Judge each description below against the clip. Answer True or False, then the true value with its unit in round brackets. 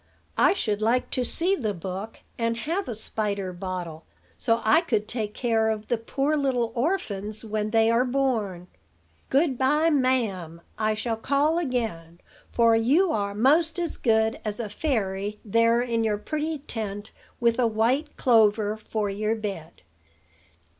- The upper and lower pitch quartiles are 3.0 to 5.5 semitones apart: True (3.8 semitones)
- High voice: True (225 Hz)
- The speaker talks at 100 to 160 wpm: True (155 wpm)